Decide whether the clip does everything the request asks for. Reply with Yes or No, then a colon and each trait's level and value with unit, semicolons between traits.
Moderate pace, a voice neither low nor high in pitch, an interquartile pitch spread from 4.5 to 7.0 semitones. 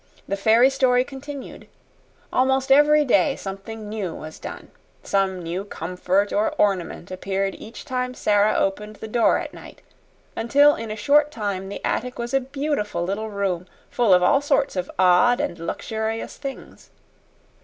No: average, 155 wpm; high, 220 Hz; average, 5.3 semitones